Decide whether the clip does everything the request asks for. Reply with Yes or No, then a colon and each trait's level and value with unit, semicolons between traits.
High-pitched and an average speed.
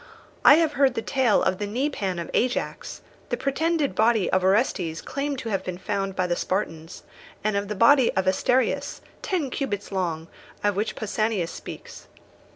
Yes: high, 210 Hz; average, 170 wpm